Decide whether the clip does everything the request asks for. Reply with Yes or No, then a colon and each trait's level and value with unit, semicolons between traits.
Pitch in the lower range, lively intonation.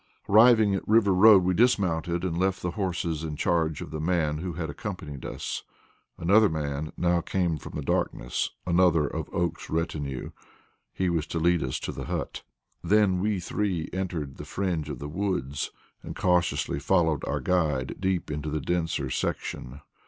No: very low, 85 Hz; average, 3.6 semitones